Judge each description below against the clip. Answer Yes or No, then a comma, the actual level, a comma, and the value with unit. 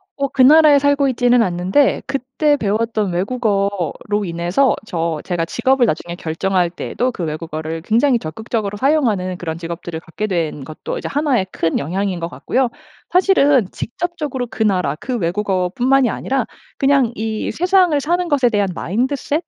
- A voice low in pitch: No, high, 220 Hz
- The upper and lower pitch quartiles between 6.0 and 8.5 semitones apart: Yes, wide, 7.4 semitones